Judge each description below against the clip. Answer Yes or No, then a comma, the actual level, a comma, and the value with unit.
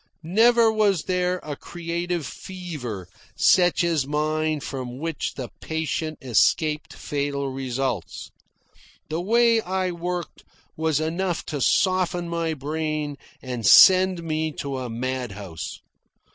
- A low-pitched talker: No, medium, 155 Hz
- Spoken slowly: Yes, slow, 120 wpm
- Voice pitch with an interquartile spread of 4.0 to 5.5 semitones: Yes, average, 4.6 semitones